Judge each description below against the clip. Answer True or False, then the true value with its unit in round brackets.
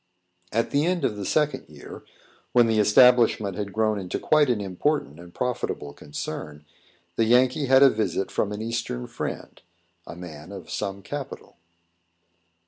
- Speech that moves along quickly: False (155 wpm)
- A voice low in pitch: True (110 Hz)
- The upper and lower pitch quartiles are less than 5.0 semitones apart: False (5.3 semitones)